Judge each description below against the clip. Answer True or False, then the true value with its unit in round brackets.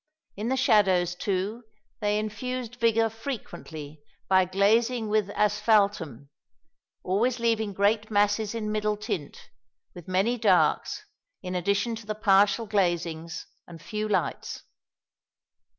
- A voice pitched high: True (210 Hz)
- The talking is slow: True (120 wpm)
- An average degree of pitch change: True (3.1 semitones)